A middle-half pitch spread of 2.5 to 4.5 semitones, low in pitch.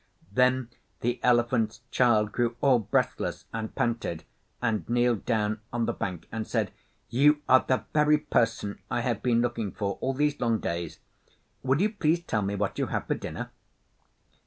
Yes: average, 3.2 semitones; low, 120 Hz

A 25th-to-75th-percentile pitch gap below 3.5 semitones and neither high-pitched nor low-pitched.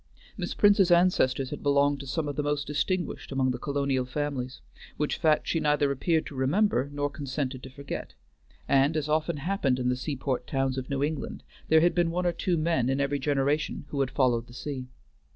Yes: average, 2.8 semitones; medium, 145 Hz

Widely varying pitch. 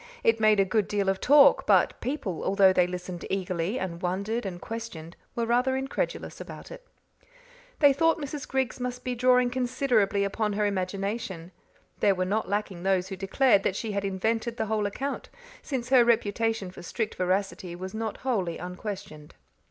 No: average, 4.5 semitones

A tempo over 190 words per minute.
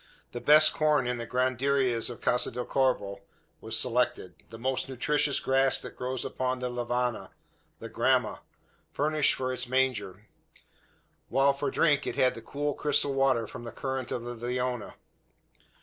No: average, 160 wpm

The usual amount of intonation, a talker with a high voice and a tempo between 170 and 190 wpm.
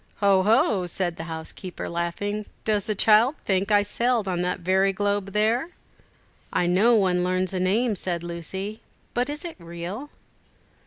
No: average, 3.2 semitones; high, 195 Hz; average, 155 wpm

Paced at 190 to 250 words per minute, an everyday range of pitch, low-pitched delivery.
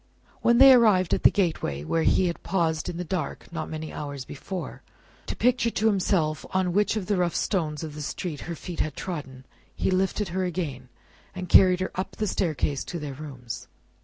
No: average, 200 wpm; average, 3.8 semitones; medium, 175 Hz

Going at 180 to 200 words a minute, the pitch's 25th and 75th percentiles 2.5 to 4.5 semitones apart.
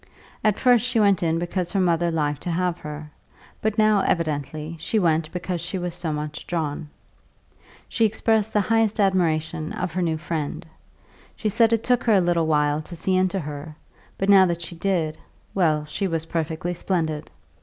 Yes: average, 185 wpm; average, 3.8 semitones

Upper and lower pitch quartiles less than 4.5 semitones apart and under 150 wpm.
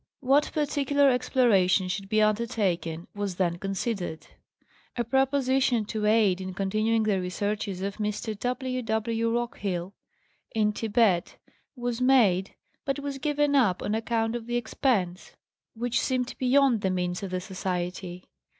No: average, 4.8 semitones; average, 140 wpm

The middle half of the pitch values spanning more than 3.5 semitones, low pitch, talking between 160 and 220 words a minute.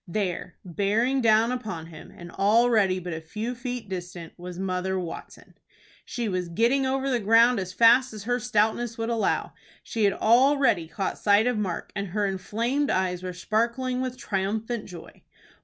No: average, 4.6 semitones; high, 215 Hz; average, 170 wpm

